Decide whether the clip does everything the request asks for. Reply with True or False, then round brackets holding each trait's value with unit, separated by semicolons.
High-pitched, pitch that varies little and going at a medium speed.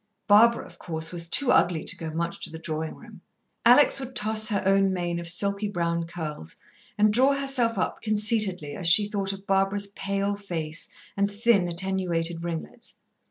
False (195 Hz; 3.8 semitones; 175 wpm)